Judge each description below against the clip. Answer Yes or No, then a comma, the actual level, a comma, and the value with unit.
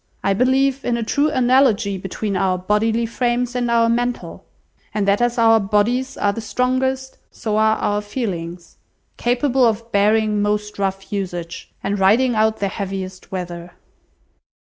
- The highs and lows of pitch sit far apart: No, average, 3.6 semitones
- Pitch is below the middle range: No, high, 220 Hz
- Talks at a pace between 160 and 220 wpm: No, average, 150 wpm